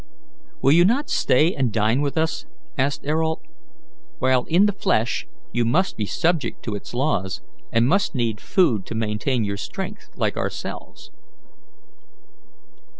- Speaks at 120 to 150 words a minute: Yes, average, 145 wpm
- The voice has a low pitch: Yes, low, 130 Hz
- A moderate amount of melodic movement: No, wide, 6.5 semitones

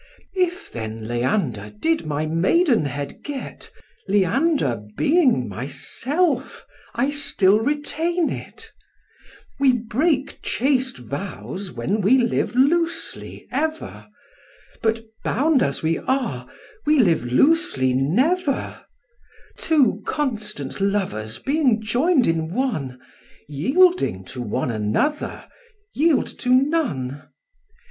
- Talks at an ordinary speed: No, slow, 100 wpm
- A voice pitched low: No, high, 235 Hz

